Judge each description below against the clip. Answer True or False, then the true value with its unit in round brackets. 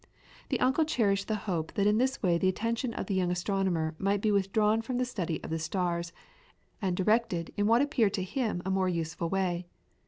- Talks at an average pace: False (210 wpm)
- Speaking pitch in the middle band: False (195 Hz)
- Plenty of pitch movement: False (3.8 semitones)